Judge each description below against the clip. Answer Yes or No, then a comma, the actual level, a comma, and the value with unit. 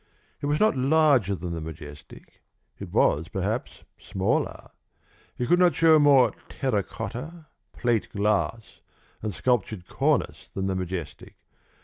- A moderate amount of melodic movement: No, wide, 7.2 semitones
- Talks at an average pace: No, slow, 130 wpm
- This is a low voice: Yes, low, 110 Hz